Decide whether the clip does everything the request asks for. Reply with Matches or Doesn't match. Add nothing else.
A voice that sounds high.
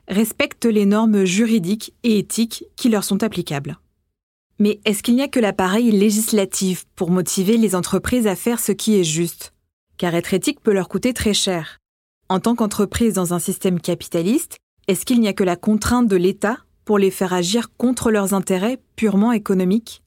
Matches